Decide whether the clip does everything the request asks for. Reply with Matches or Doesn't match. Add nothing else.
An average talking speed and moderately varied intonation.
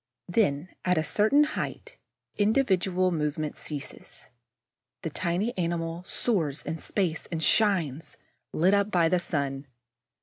Doesn't match